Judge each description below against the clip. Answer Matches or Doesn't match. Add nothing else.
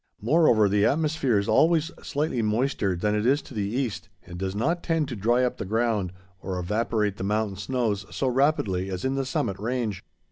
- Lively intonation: Doesn't match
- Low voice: Matches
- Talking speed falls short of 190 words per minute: Doesn't match